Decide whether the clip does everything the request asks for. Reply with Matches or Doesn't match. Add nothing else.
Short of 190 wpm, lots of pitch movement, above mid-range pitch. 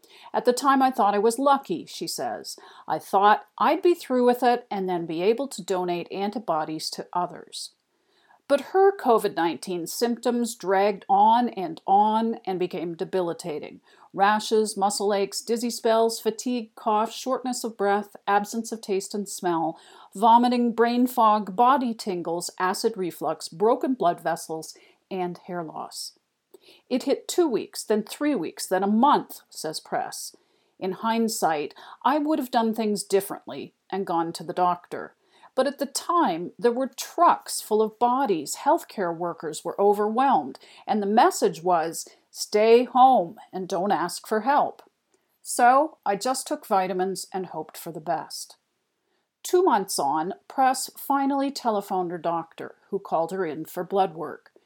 Matches